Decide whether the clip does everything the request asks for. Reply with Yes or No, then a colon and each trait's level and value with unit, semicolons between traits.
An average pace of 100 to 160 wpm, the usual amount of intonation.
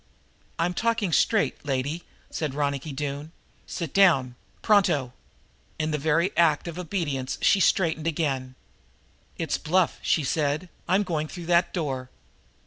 Yes: slow, 135 wpm; average, 3.7 semitones